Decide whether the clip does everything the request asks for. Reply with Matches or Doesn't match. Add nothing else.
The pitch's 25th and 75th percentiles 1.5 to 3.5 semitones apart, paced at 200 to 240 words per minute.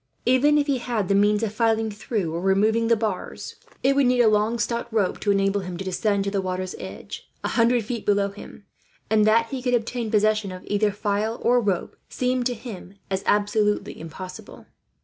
Matches